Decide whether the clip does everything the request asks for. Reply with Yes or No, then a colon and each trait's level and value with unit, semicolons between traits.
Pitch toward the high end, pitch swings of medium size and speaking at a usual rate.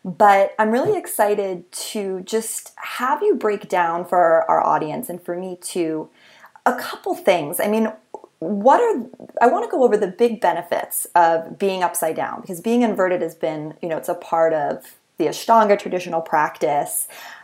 Yes: high, 195 Hz; average, 4.3 semitones; average, 175 wpm